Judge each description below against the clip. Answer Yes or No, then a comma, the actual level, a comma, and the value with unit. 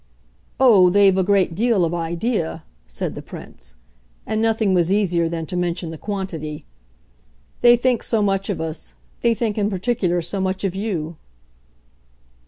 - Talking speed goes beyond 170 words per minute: No, average, 160 wpm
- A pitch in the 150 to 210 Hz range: Yes, high, 190 Hz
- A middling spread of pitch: Yes, average, 3.9 semitones